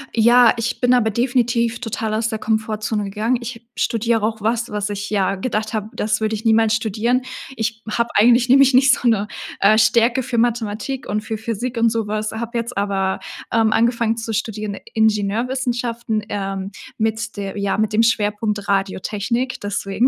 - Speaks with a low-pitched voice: No, high, 220 Hz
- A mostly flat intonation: Yes, narrow, 2.0 semitones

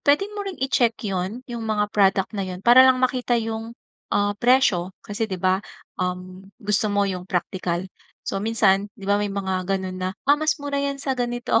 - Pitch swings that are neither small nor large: Yes, average, 4.7 semitones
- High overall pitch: Yes, high, 210 Hz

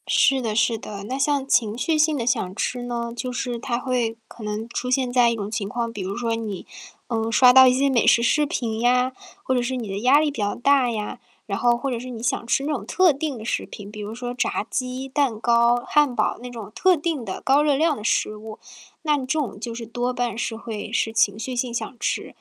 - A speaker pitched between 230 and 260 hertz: Yes, high, 240 Hz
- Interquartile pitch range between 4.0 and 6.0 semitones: No, average, 2.8 semitones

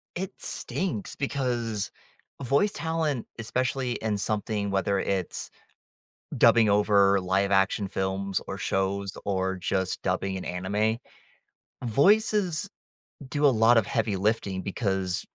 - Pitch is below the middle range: Yes, low, 105 Hz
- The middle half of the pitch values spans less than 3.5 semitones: No, average, 4.4 semitones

